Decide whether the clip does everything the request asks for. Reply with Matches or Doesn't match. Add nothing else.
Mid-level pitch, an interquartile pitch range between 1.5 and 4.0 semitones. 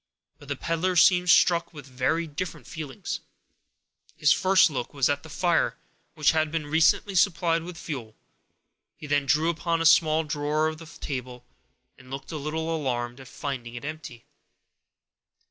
Matches